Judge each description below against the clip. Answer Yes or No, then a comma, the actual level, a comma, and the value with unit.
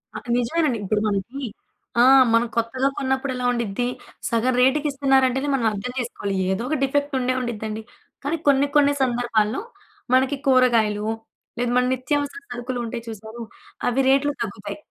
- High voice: Yes, very high, 250 Hz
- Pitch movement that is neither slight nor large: Yes, average, 3.0 semitones